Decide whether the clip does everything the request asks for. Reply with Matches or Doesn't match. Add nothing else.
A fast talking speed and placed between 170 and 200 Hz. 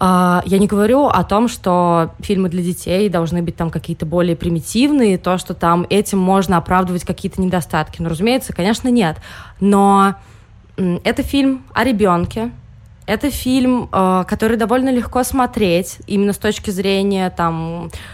Doesn't match